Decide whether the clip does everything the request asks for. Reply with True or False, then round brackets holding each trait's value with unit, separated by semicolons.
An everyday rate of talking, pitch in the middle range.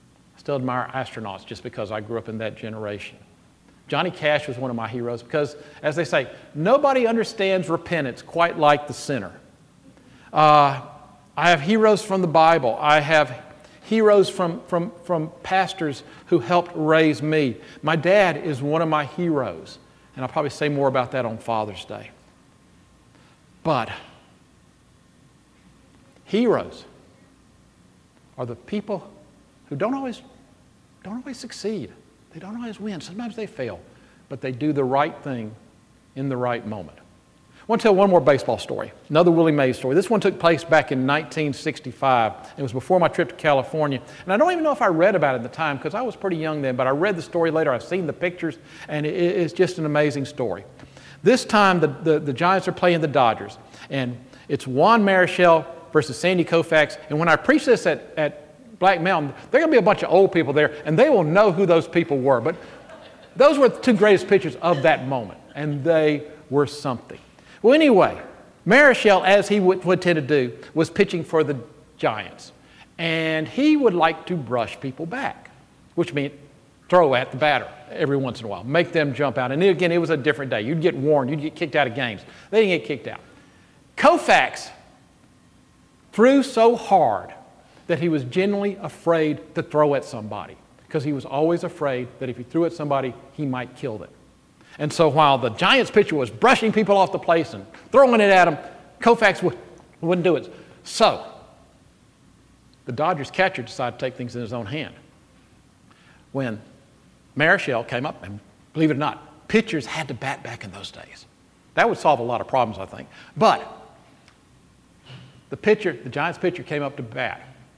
True (190 wpm; 155 Hz)